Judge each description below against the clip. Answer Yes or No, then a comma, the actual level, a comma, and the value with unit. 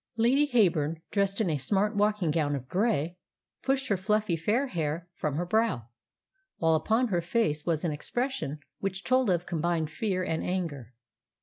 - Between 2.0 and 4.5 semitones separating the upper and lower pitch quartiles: No, wide, 5.5 semitones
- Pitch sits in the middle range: Yes, medium, 180 Hz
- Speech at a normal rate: Yes, average, 170 wpm